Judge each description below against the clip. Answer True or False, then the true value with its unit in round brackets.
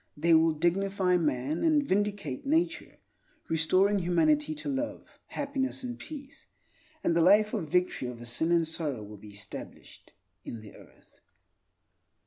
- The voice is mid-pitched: True (180 Hz)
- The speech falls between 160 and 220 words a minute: False (140 wpm)